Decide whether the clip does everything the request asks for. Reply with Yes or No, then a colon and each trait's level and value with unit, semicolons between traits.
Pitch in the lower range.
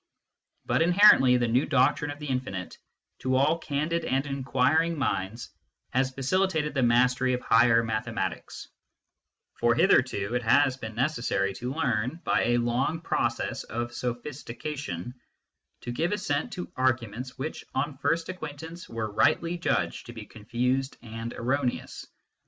Yes: low, 130 Hz